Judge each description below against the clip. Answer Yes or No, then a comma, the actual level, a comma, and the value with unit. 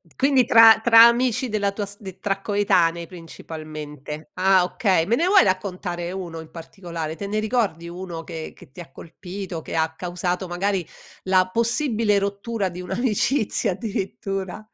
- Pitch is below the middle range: No, high, 190 Hz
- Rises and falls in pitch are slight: No, average, 3.9 semitones